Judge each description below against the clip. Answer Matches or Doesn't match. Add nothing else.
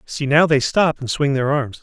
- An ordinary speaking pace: Doesn't match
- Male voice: Matches